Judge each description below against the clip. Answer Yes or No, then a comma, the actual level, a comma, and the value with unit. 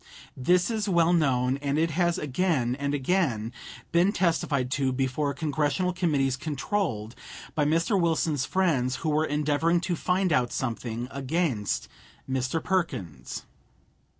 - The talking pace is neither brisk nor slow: No, slow, 130 wpm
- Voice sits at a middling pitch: Yes, medium, 150 Hz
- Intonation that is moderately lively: Yes, average, 4.7 semitones